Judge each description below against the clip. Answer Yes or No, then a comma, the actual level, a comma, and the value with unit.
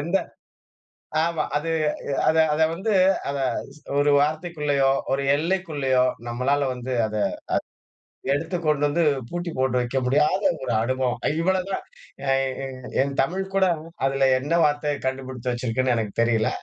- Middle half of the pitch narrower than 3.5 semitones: No, average, 3.8 semitones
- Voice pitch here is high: No, medium, 140 Hz